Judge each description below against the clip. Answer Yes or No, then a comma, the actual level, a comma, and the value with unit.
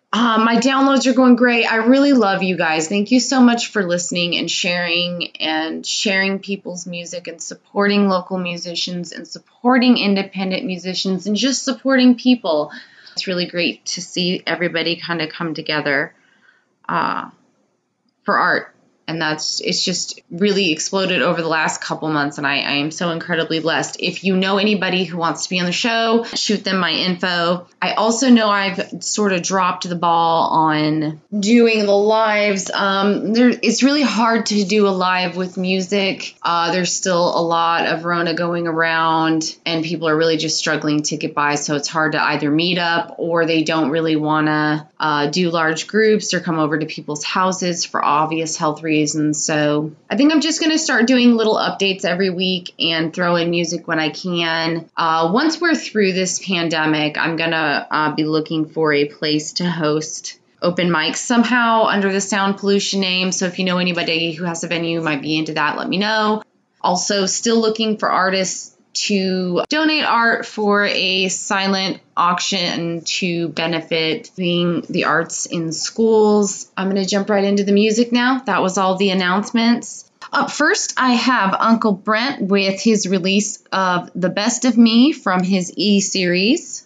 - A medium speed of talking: Yes, average, 180 wpm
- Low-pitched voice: No, medium, 185 Hz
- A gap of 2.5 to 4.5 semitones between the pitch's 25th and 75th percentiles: Yes, average, 4.1 semitones